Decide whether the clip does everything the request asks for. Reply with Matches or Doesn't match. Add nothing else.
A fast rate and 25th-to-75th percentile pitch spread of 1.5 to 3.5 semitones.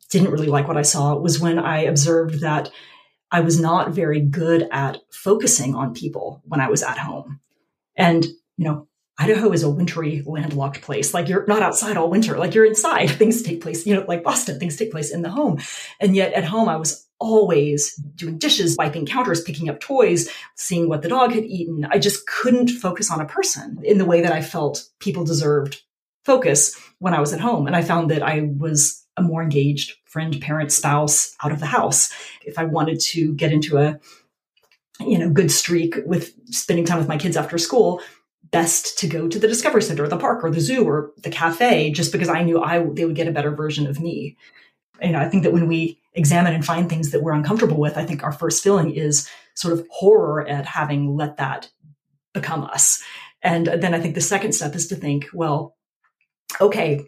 Matches